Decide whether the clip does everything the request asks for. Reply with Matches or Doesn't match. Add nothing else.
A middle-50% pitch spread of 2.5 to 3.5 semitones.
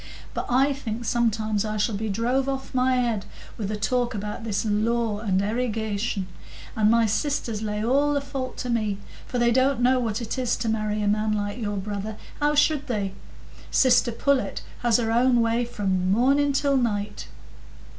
Matches